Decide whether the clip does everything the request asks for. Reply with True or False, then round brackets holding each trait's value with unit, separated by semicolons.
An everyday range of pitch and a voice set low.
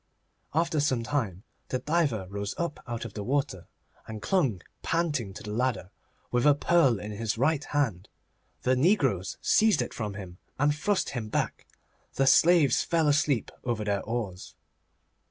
False (5.9 semitones; 125 Hz)